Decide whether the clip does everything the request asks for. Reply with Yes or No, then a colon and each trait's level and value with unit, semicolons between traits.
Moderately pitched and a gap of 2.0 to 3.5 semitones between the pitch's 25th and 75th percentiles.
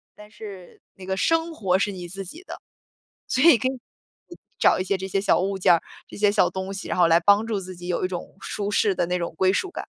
No: high, 195 Hz; narrow, 2.4 semitones